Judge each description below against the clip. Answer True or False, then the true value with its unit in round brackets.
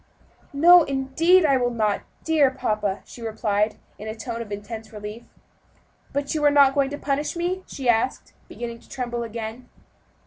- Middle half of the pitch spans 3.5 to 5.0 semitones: True (4.4 semitones)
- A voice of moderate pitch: False (245 Hz)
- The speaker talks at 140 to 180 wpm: True (170 wpm)